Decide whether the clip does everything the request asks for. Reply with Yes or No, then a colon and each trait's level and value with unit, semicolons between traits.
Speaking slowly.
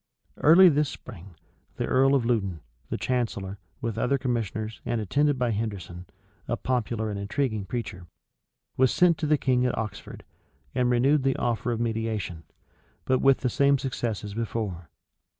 No: average, 165 wpm